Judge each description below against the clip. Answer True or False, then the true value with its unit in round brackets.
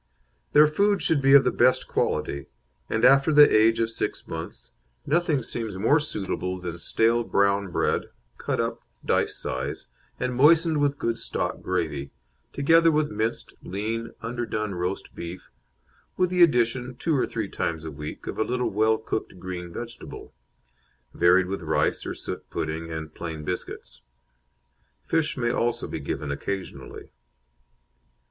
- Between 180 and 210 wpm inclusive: False (150 wpm)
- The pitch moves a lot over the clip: True (7.3 semitones)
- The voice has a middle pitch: False (115 Hz)